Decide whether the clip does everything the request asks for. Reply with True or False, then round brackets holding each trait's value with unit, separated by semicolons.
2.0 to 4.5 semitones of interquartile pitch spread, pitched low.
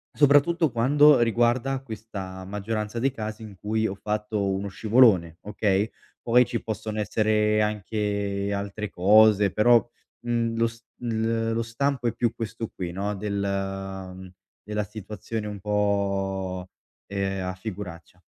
True (2.7 semitones; 105 Hz)